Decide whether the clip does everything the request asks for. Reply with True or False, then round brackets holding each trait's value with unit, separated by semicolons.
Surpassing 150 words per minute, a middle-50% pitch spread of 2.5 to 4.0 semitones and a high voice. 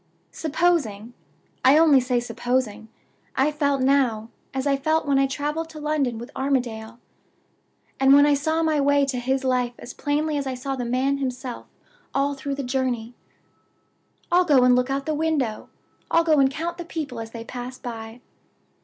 True (180 wpm; 3.0 semitones; 270 Hz)